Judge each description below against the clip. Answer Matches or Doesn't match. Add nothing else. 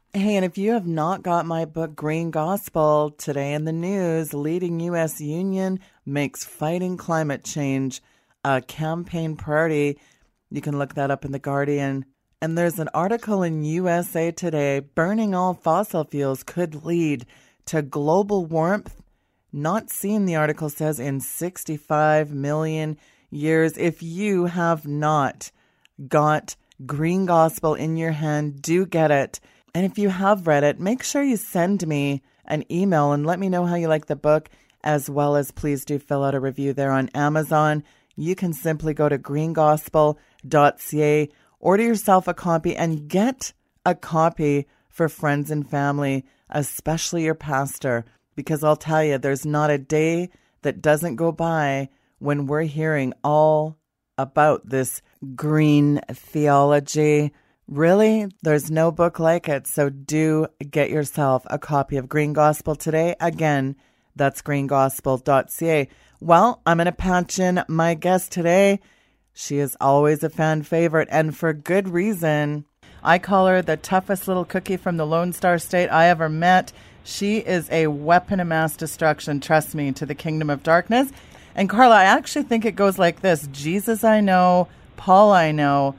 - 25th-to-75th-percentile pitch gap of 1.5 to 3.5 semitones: Matches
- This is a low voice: Doesn't match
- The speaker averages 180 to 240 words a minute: Doesn't match